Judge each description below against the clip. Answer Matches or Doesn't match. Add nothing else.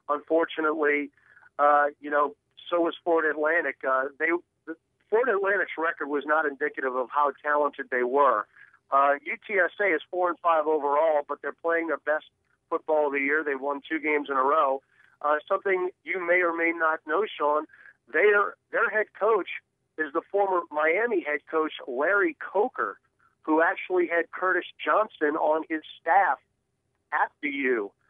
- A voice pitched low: Doesn't match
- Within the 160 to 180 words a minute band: Matches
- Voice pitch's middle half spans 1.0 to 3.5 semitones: Matches